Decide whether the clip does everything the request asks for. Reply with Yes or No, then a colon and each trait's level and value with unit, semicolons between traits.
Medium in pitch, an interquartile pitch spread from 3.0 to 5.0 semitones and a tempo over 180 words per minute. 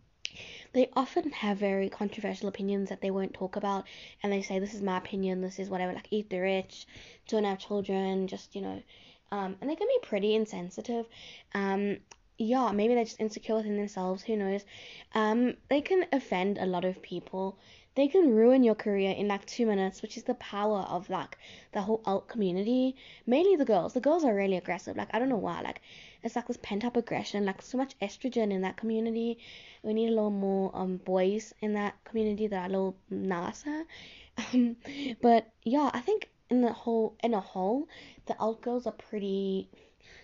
No: high, 210 Hz; average, 3.5 semitones; average, 200 wpm